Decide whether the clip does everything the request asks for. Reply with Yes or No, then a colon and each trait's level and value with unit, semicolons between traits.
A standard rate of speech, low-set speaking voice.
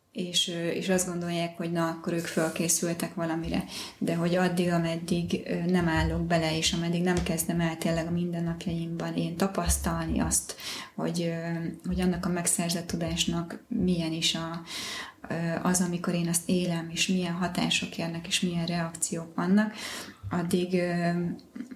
No: average, 140 wpm; medium, 170 Hz